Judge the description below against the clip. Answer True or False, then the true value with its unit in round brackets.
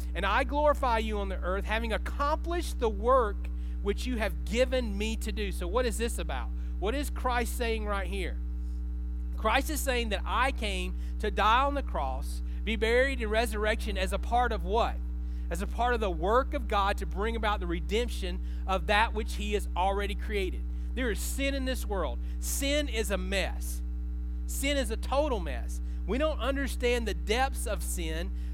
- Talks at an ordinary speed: True (190 wpm)